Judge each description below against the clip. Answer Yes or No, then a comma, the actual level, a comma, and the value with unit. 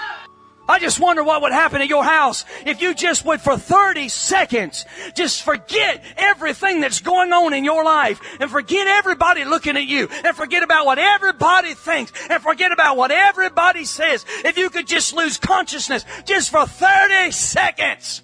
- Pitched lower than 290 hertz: No, very high, 330 Hz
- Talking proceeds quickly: No, average, 175 wpm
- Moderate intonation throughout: Yes, average, 3.7 semitones